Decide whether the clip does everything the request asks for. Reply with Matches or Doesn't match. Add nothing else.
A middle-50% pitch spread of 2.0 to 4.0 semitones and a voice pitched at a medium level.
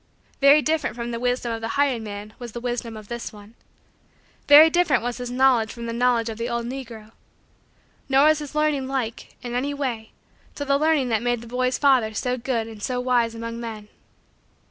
Doesn't match